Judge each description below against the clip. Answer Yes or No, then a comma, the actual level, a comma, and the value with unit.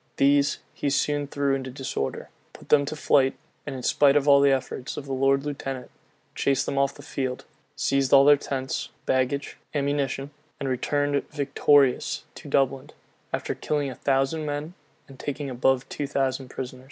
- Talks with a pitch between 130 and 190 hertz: Yes, medium, 140 Hz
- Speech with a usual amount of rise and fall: No, narrow, 1.3 semitones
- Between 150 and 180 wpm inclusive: Yes, average, 165 wpm